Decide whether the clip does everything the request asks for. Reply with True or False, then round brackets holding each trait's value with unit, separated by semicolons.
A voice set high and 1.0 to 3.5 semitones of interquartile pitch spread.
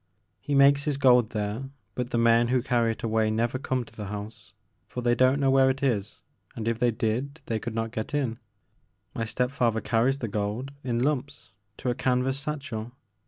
False (120 Hz; 3.0 semitones)